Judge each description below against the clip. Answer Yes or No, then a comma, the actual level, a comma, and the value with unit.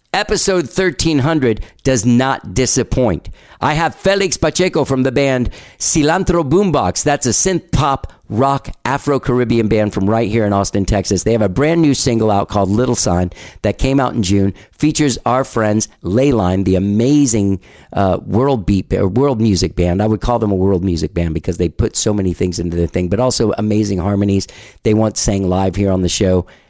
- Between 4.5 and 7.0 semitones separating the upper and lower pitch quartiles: Yes, wide, 5.6 semitones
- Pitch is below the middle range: Yes, low, 110 Hz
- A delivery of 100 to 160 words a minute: No, average, 195 wpm